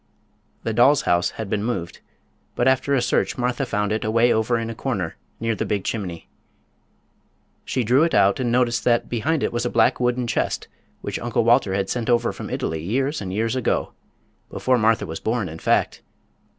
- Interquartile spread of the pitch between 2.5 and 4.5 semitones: Yes, average, 3.0 semitones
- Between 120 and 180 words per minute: No, average, 190 wpm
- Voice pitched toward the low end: Yes, low, 115 Hz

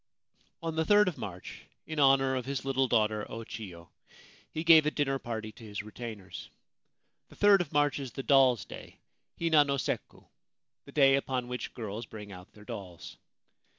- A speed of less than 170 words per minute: No, average, 185 wpm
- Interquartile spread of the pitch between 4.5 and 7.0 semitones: Yes, average, 5.2 semitones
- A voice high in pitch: No, low, 130 Hz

